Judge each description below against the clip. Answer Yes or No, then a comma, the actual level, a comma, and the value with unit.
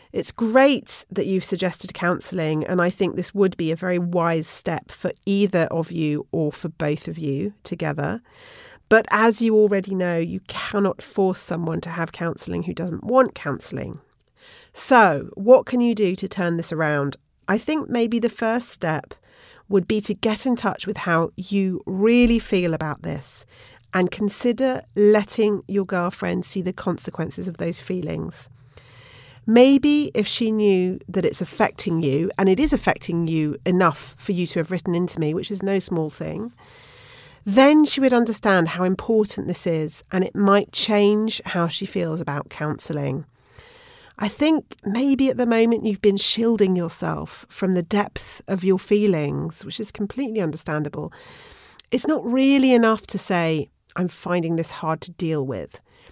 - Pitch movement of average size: Yes, average, 4.7 semitones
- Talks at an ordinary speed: Yes, average, 170 wpm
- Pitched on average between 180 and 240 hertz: Yes, high, 190 Hz